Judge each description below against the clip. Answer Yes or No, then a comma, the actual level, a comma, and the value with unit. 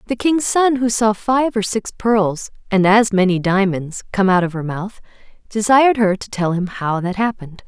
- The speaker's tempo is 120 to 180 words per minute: No, fast, 205 wpm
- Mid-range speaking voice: No, high, 205 Hz